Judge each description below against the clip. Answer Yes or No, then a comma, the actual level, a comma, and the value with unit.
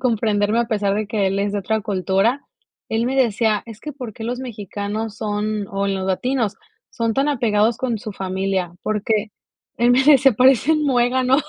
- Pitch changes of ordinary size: Yes, average, 3.5 semitones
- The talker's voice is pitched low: No, high, 220 Hz